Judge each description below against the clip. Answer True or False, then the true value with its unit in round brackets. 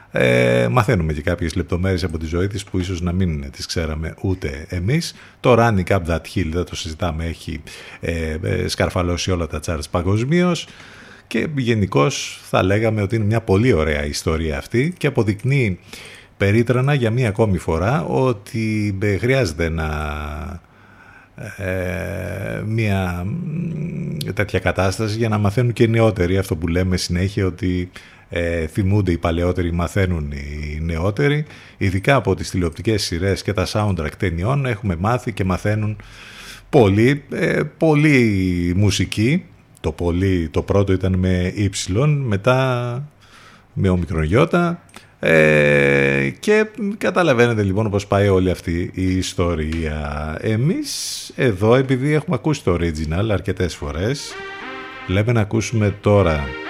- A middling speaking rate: True (135 wpm)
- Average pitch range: True (5.0 semitones)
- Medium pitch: False (95 Hz)